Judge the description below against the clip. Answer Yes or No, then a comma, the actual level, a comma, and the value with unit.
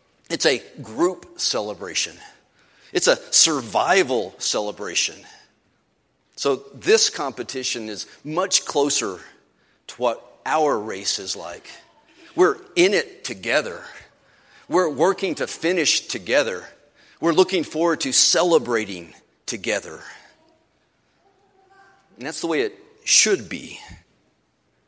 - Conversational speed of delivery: No, slow, 100 wpm